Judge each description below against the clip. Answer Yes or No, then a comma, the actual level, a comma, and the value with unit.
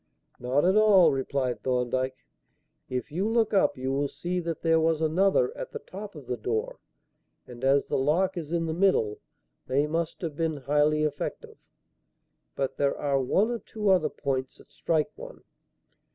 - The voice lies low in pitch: No, medium, 150 Hz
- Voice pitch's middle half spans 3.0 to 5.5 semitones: Yes, average, 5.2 semitones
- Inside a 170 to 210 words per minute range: Yes, average, 175 wpm